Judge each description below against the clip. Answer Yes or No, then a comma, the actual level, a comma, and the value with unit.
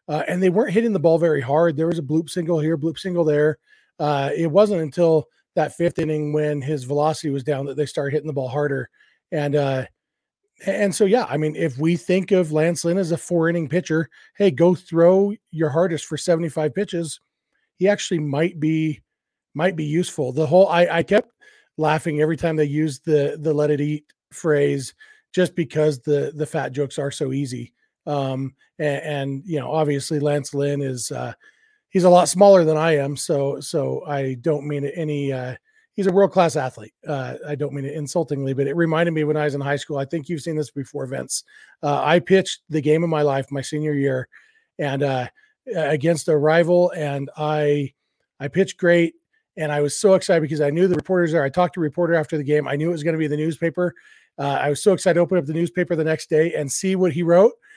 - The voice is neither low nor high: Yes, medium, 155 Hz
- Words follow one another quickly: Yes, fast, 220 wpm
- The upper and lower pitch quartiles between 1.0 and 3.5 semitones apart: Yes, average, 3.1 semitones